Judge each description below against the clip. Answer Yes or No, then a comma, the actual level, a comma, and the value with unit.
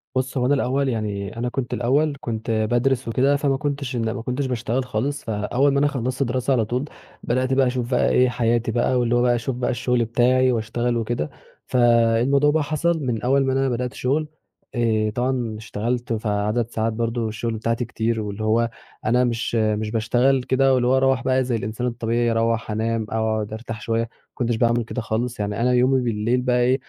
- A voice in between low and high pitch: No, low, 120 Hz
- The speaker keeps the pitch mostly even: Yes, narrow, 2.3 semitones